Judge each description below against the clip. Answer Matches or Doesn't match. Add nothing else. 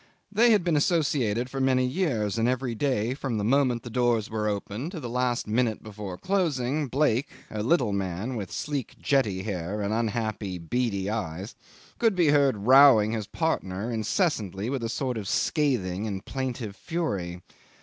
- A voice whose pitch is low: Matches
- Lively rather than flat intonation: Doesn't match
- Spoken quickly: Doesn't match